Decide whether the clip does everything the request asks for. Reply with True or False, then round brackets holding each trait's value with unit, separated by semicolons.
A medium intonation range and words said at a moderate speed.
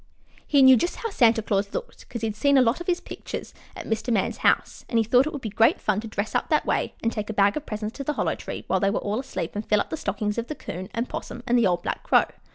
False (4.0 semitones; 290 wpm)